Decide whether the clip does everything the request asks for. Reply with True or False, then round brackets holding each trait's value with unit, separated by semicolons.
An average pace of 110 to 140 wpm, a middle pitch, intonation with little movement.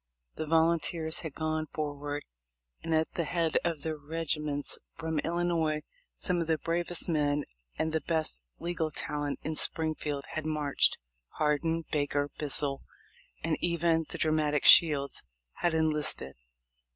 True (135 wpm; 155 Hz; 1.8 semitones)